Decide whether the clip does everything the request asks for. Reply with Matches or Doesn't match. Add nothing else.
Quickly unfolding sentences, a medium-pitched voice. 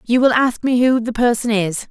Doesn't match